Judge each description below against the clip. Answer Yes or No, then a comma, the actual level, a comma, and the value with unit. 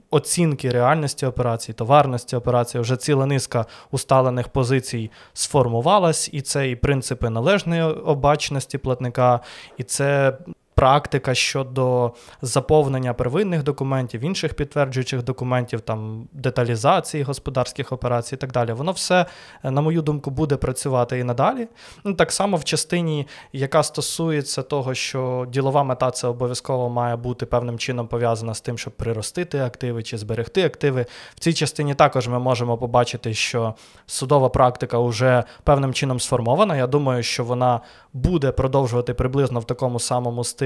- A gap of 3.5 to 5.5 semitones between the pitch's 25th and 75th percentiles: No, average, 2.9 semitones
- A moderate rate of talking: Yes, average, 140 wpm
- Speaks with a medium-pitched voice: No, low, 130 Hz